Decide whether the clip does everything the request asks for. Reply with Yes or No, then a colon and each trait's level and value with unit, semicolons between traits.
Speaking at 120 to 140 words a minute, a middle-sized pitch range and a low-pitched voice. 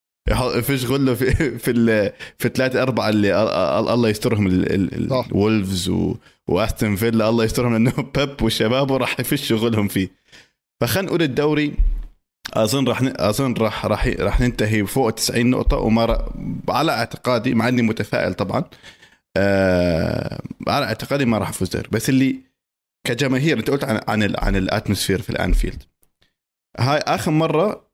Yes: fast, 135 wpm; average, 3.8 semitones; low, 115 Hz